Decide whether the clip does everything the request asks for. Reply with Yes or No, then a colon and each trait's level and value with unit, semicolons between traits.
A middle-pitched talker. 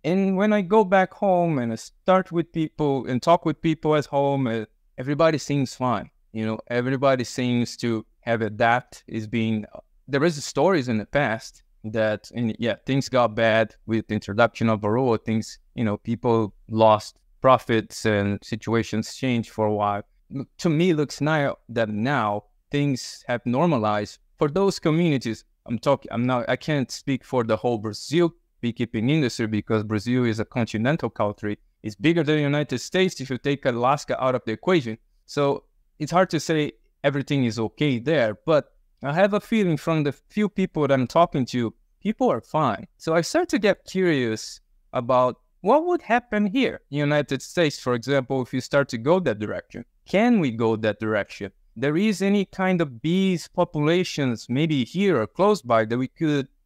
No: low, 130 Hz